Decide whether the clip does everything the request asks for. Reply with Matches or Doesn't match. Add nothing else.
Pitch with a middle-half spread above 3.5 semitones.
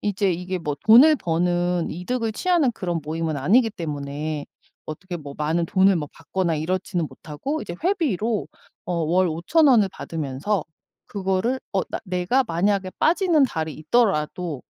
Matches